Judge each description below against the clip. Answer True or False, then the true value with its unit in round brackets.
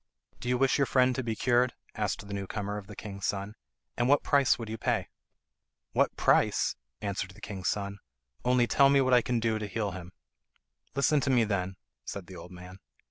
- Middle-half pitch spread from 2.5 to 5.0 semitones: True (4.1 semitones)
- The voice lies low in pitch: True (110 Hz)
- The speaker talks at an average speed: False (210 wpm)